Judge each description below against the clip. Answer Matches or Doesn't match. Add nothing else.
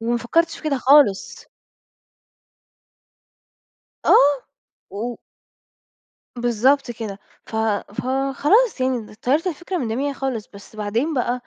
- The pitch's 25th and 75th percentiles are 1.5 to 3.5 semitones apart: Doesn't match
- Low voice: Doesn't match